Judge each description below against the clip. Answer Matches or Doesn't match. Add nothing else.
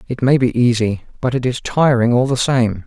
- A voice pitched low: Matches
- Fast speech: Matches